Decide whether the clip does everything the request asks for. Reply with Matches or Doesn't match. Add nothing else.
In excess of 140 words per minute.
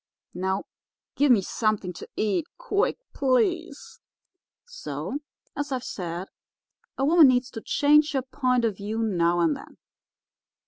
Doesn't match